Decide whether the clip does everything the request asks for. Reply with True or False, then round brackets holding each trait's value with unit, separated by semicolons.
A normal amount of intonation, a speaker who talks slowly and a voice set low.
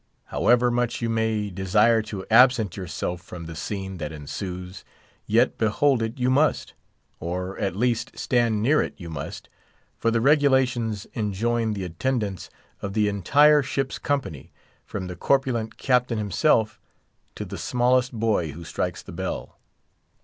False (4.8 semitones; 150 wpm; 110 Hz)